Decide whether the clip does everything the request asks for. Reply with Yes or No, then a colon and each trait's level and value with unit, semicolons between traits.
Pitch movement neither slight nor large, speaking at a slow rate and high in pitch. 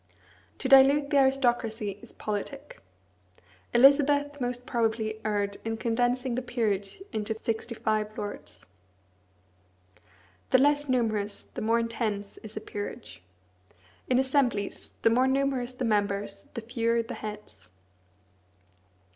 Yes: average, 3.5 semitones; slow, 120 wpm; high, 230 Hz